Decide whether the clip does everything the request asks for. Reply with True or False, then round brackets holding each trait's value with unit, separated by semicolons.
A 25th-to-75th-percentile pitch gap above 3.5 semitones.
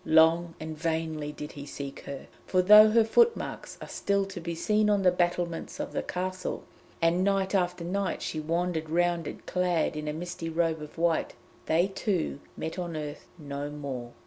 False (2.8 semitones)